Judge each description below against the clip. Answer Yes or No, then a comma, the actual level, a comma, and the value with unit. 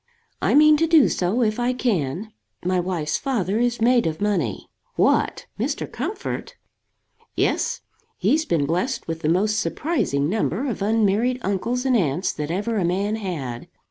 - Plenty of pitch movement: Yes, wide, 6.1 semitones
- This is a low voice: No, high, 205 Hz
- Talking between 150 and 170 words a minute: Yes, average, 160 wpm